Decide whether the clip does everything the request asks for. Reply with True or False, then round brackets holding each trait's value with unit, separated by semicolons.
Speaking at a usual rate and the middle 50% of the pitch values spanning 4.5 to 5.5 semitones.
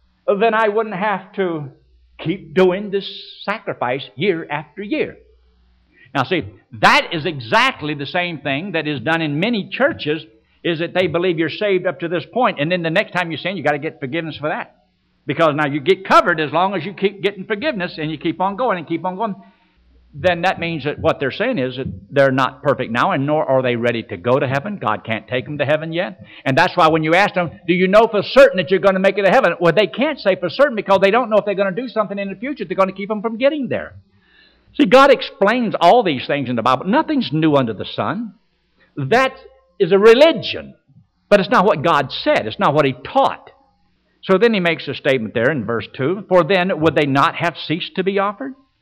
False (240 wpm; 4.9 semitones)